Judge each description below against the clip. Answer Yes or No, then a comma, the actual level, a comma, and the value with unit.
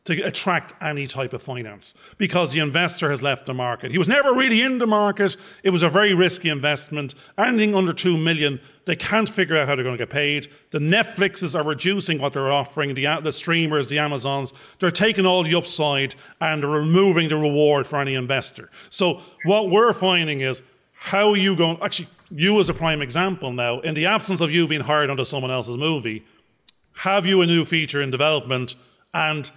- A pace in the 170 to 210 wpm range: Yes, average, 200 wpm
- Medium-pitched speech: Yes, medium, 155 Hz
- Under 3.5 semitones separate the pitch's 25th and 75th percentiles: No, average, 4.7 semitones